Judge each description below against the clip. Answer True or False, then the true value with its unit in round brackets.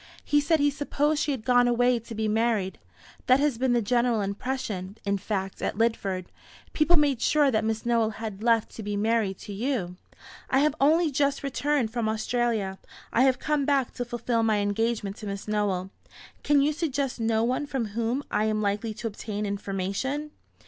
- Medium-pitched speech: False (230 Hz)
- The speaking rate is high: False (190 wpm)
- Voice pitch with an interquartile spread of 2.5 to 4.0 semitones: False (4.4 semitones)